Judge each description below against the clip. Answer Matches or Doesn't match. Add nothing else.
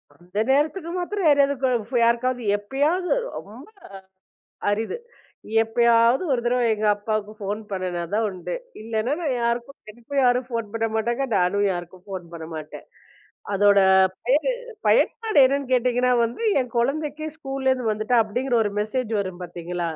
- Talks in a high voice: Matches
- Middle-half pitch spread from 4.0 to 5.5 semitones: Matches